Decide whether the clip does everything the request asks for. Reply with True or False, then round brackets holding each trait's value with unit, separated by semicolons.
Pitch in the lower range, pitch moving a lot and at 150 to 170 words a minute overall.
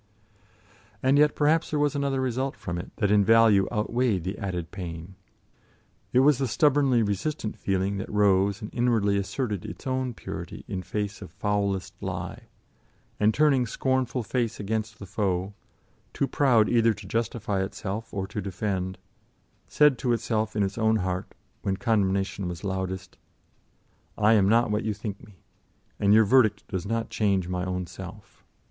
False (105 Hz; 3.7 semitones; 165 wpm)